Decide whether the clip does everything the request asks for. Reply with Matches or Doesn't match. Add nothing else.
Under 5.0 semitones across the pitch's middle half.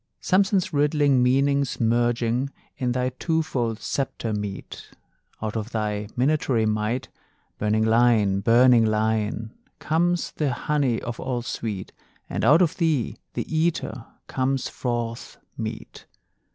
Matches